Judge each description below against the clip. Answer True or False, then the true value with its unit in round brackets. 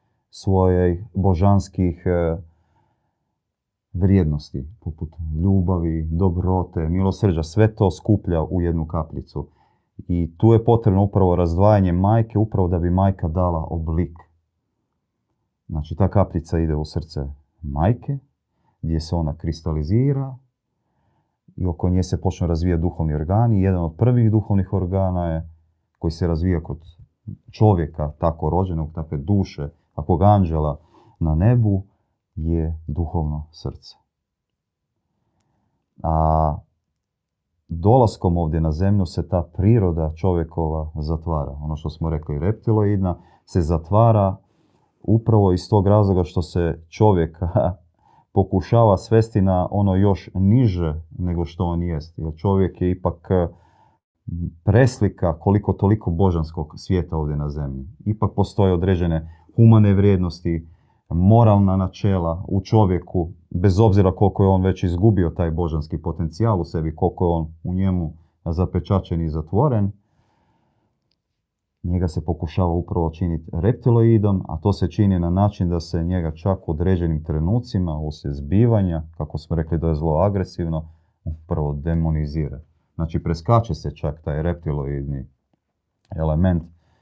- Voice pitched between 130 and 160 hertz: False (90 Hz)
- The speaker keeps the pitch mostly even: False (3.5 semitones)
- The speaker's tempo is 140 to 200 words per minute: False (125 wpm)